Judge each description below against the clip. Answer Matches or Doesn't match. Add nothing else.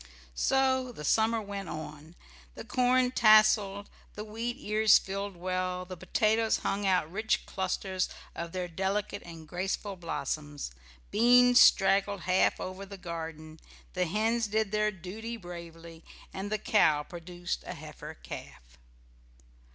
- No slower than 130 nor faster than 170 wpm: Matches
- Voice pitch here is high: Matches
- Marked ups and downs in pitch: Doesn't match